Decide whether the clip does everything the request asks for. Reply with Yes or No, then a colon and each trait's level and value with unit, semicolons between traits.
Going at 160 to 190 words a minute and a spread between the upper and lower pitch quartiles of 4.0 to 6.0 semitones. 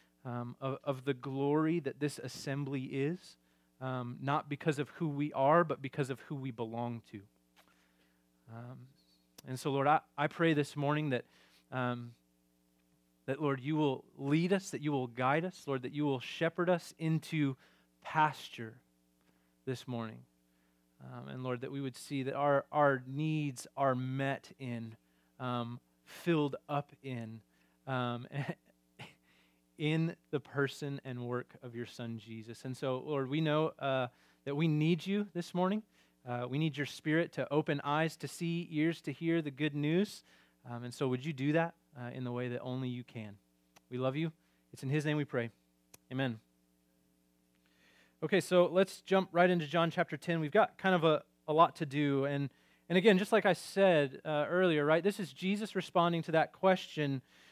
Yes: average, 180 wpm; average, 5.0 semitones